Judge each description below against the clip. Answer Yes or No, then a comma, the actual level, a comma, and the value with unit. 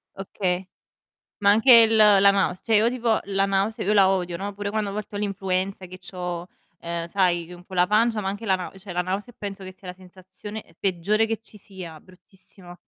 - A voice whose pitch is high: Yes, high, 195 Hz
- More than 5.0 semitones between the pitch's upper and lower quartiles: No, narrow, 2.3 semitones